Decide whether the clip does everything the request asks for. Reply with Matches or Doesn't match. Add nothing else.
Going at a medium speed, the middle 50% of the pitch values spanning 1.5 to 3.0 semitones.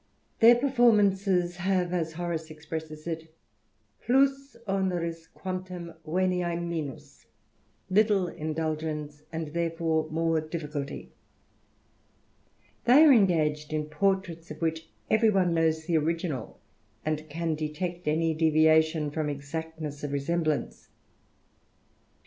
Doesn't match